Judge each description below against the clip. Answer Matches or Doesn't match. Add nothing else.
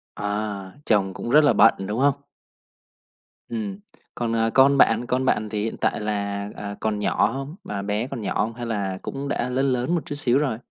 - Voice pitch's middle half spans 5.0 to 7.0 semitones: Doesn't match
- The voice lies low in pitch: Matches